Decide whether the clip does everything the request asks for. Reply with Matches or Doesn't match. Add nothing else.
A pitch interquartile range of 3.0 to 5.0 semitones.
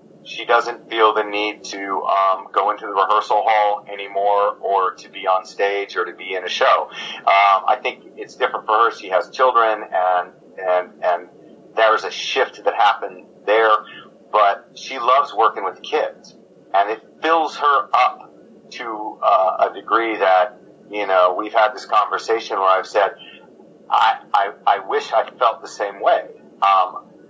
Doesn't match